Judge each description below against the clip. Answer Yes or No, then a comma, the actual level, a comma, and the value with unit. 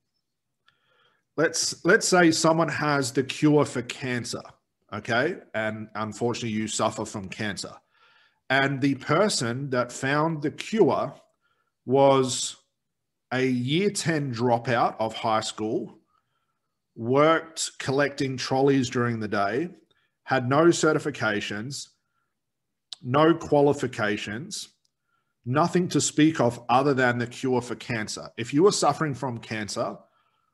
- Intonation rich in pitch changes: No, average, 4.3 semitones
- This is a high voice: No, low, 130 Hz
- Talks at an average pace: No, slow, 115 wpm